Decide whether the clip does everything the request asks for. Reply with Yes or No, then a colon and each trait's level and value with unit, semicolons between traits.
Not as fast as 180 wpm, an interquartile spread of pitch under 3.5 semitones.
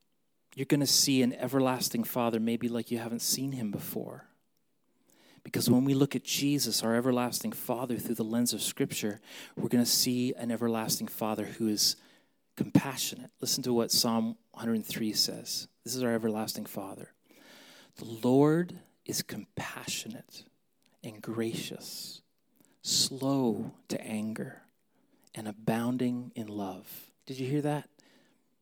Yes: average, 140 wpm; average, 3.1 semitones